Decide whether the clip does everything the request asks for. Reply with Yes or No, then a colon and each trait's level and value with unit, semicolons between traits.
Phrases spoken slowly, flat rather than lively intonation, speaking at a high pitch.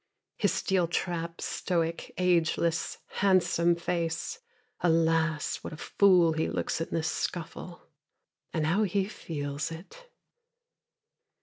No: slow, 110 wpm; narrow, 2.0 semitones; medium, 170 Hz